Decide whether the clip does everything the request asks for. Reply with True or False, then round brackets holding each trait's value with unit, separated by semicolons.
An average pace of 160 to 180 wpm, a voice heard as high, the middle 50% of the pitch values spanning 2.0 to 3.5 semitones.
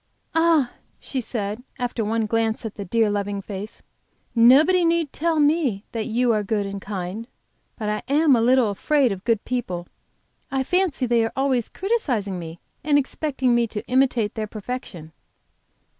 False (165 wpm; 235 Hz; 4.6 semitones)